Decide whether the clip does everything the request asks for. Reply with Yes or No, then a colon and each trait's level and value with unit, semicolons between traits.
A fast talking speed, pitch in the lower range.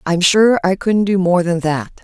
No: fast, 235 wpm; medium, 185 Hz